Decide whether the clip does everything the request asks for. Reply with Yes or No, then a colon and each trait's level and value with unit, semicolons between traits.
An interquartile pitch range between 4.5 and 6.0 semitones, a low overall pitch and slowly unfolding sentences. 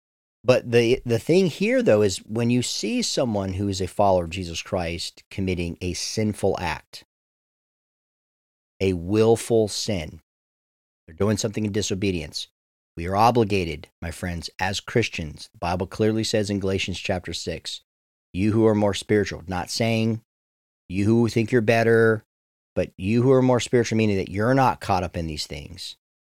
No: average, 5.0 semitones; low, 100 Hz; average, 165 wpm